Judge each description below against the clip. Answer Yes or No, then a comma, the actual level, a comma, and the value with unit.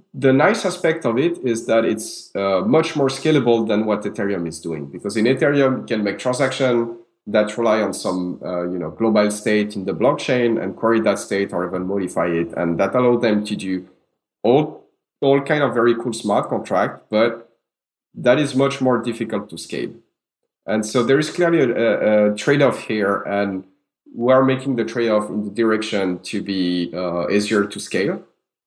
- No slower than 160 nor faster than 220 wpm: Yes, average, 190 wpm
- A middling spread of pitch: Yes, average, 4.2 semitones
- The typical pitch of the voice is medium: No, low, 110 Hz